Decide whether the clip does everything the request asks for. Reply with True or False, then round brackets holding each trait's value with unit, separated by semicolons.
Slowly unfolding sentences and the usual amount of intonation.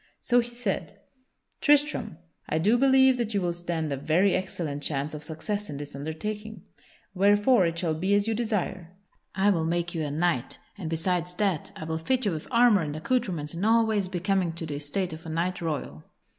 False (200 wpm; 4.7 semitones)